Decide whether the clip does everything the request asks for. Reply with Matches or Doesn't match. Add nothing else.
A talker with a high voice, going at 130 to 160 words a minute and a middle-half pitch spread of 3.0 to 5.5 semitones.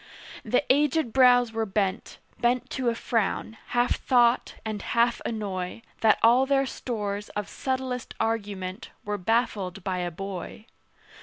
Matches